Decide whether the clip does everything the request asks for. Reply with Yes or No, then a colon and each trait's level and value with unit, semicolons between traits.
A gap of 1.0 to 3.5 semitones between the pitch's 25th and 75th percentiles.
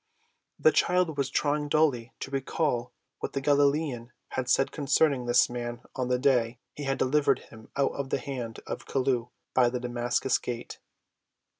Yes: average, 2.8 semitones